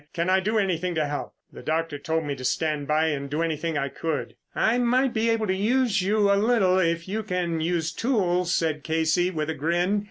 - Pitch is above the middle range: No, medium, 175 Hz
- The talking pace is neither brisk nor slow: No, fast, 220 wpm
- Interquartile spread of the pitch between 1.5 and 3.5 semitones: No, average, 4.2 semitones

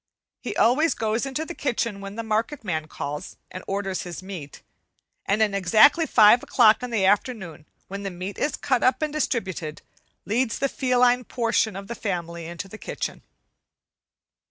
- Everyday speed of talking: Yes, average, 170 wpm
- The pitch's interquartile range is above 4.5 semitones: Yes, average, 4.9 semitones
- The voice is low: No, high, 215 Hz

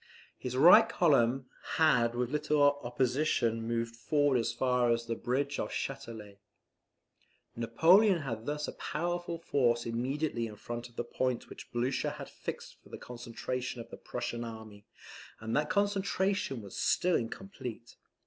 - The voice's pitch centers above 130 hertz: No, low, 125 Hz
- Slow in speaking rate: No, average, 150 wpm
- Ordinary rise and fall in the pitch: Yes, average, 4.3 semitones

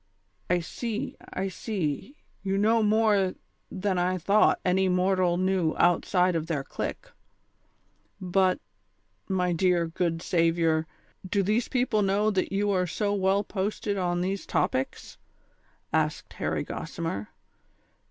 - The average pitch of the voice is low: No, medium, 185 Hz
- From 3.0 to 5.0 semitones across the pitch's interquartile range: No, narrow, 2.6 semitones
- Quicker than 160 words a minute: No, slow, 135 wpm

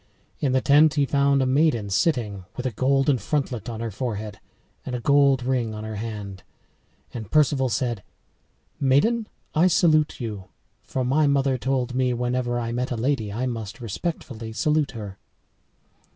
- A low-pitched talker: Yes, low, 125 Hz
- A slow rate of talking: No, average, 165 wpm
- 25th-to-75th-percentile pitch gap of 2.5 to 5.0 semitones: Yes, average, 3.9 semitones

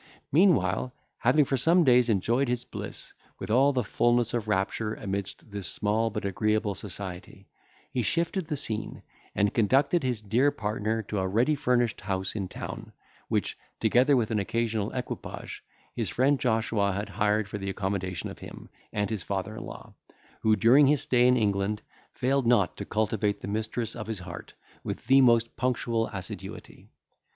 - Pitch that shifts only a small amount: No, average, 3.6 semitones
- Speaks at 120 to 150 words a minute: No, average, 170 wpm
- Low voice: Yes, low, 110 Hz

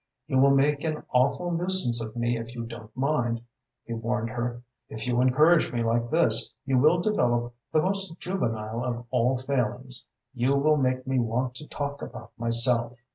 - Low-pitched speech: Yes, low, 125 Hz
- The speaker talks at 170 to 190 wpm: Yes, average, 180 wpm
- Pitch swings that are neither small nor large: Yes, average, 3.2 semitones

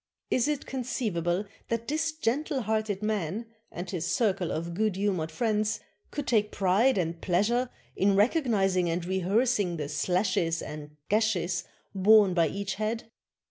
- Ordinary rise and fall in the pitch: Yes, average, 4.4 semitones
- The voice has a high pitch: Yes, high, 200 Hz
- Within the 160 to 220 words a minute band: No, average, 145 wpm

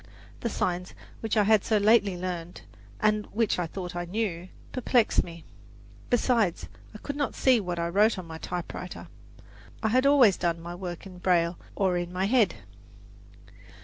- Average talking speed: Yes, average, 170 wpm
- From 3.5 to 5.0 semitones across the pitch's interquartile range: Yes, average, 4.0 semitones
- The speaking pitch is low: No, high, 190 Hz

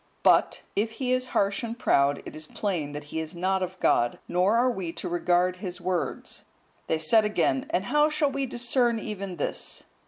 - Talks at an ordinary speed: Yes, average, 195 wpm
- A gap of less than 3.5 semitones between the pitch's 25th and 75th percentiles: No, average, 5.3 semitones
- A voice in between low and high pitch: No, high, 195 Hz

